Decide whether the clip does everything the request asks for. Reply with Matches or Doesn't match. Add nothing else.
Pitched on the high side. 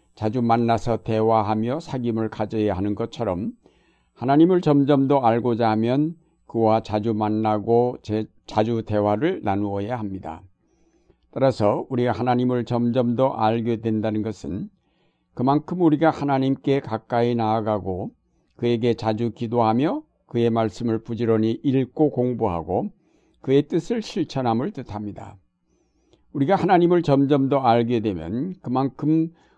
Doesn't match